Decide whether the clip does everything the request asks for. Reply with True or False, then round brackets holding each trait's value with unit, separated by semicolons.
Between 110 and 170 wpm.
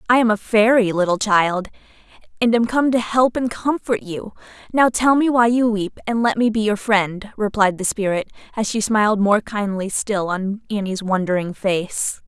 False (190 wpm)